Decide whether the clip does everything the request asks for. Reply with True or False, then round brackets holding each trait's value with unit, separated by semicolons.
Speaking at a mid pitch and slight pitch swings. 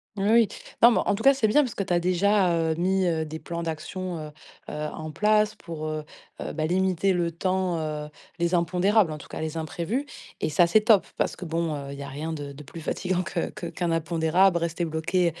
False (170 Hz; 3.0 semitones)